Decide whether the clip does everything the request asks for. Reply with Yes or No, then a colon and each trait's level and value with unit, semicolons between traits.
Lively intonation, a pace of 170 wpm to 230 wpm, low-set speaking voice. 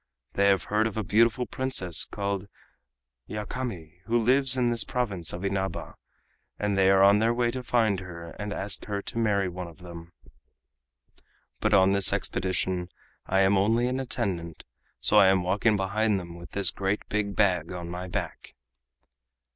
No: average, 3.3 semitones; average, 175 wpm; low, 100 Hz